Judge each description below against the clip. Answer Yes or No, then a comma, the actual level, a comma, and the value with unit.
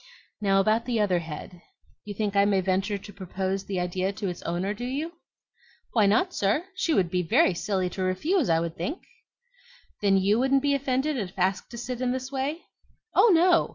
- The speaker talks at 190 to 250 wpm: Yes, average, 195 wpm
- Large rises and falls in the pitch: Yes, wide, 5.8 semitones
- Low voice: No, high, 205 Hz